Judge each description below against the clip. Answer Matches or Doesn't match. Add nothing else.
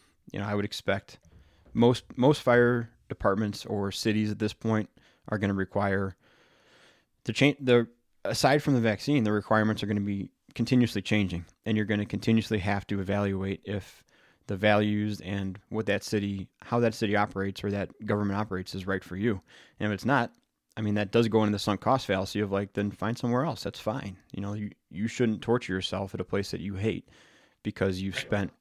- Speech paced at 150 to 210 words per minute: Matches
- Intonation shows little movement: Matches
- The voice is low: Matches